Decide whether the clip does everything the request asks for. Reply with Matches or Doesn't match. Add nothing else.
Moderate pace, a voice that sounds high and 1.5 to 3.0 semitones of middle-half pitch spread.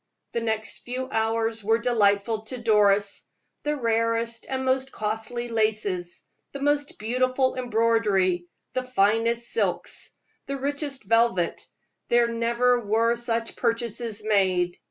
Doesn't match